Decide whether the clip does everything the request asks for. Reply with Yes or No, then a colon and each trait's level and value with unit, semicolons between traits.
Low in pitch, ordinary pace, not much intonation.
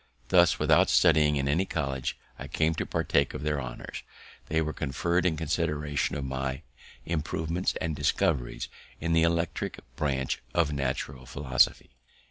No: very low, 75 Hz; average, 145 wpm; average, 3.3 semitones